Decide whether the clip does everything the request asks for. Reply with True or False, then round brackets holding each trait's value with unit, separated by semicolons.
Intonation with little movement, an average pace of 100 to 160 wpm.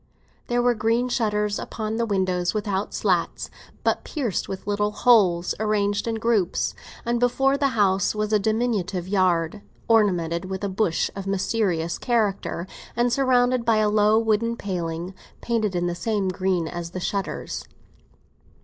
False (3.5 semitones; 150 wpm)